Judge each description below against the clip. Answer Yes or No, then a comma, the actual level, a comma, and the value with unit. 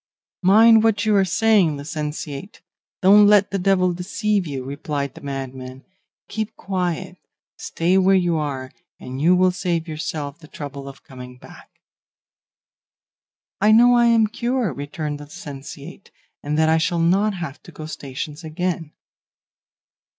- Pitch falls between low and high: Yes, medium, 170 Hz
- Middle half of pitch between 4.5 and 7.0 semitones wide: Yes, average, 5.3 semitones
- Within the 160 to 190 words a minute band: No, average, 145 wpm